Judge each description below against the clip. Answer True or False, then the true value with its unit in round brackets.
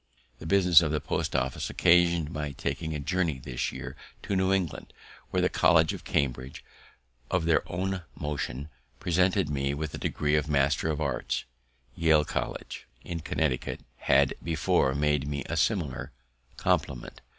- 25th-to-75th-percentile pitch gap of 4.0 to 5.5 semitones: False (3.3 semitones)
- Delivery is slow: False (155 wpm)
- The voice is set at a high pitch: False (75 Hz)